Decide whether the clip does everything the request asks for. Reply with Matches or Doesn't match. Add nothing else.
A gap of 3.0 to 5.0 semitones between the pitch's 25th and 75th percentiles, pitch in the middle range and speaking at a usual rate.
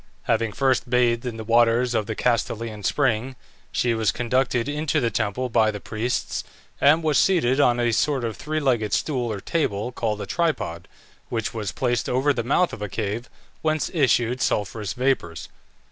Doesn't match